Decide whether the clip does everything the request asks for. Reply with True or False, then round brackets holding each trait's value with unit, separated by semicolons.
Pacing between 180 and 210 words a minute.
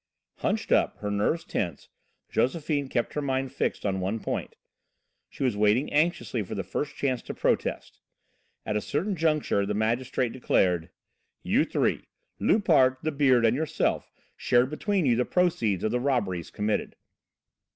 False (155 wpm)